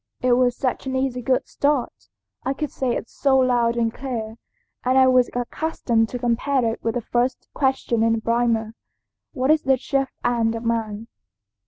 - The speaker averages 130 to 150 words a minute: No, average, 185 wpm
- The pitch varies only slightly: Yes, narrow, 2.3 semitones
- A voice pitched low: No, high, 245 Hz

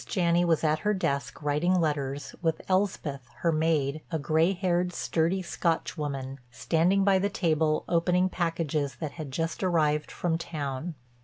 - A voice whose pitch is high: No, medium, 165 Hz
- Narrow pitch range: No, average, 3.0 semitones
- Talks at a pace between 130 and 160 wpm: Yes, average, 155 wpm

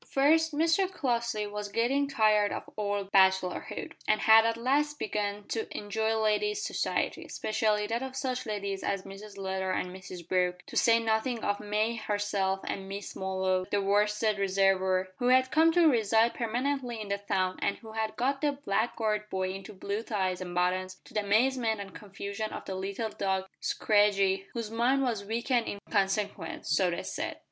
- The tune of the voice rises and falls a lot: No, average, 3.2 semitones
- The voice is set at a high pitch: Yes, high, 210 Hz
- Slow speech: No, average, 175 wpm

